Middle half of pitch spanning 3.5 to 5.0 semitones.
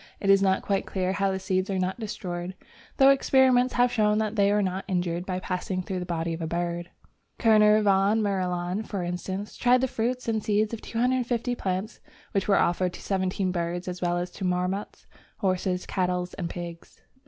No: average, 2.9 semitones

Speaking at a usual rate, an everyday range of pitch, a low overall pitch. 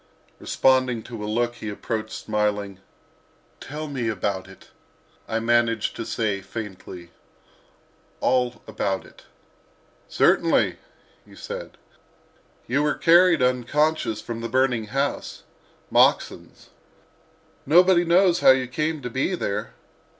No: slow, 110 wpm; average, 4.7 semitones; low, 120 Hz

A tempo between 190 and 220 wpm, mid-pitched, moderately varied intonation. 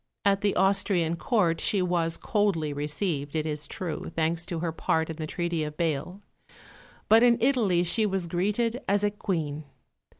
No: average, 170 wpm; medium, 175 Hz; average, 4.1 semitones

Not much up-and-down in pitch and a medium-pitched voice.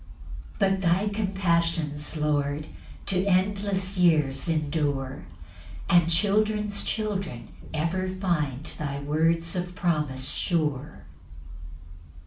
No: average, 4.2 semitones; medium, 170 Hz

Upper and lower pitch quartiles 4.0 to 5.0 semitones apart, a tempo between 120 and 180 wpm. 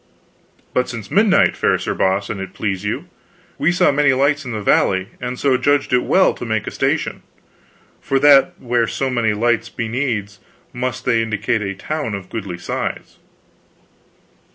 Yes: average, 4.5 semitones; average, 175 wpm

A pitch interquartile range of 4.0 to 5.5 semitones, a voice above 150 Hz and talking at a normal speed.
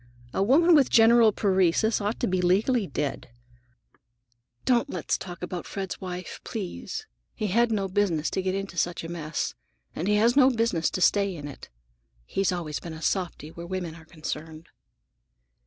Yes: average, 4.5 semitones; medium, 185 Hz; average, 175 wpm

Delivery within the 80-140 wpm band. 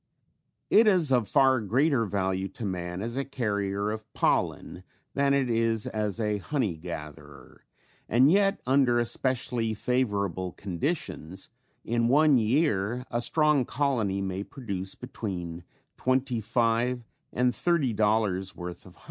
Yes: slow, 135 wpm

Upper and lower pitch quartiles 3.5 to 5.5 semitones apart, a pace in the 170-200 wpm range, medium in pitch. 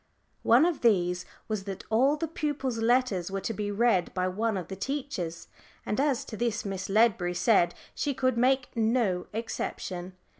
No: average, 5.2 semitones; average, 175 wpm; high, 220 Hz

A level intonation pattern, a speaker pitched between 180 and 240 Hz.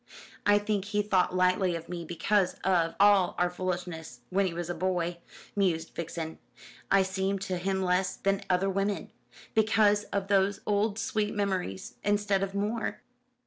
Yes: narrow, 2.3 semitones; high, 190 Hz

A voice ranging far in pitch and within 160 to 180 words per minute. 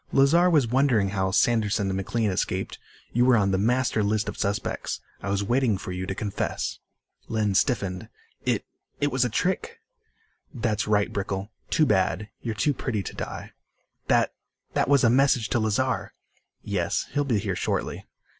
No: average, 4.5 semitones; average, 170 wpm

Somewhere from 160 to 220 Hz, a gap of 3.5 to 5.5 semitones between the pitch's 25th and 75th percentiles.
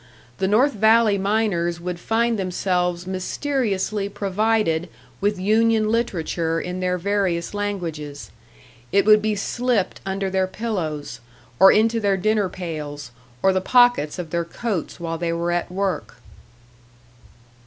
Yes: high, 190 Hz; average, 3.8 semitones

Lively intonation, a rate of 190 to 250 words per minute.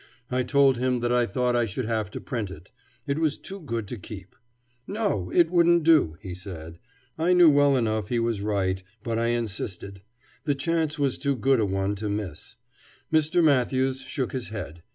Yes: wide, 5.9 semitones; average, 195 wpm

